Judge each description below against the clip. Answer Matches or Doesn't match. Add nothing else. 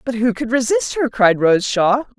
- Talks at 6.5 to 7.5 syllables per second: Doesn't match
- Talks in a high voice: Matches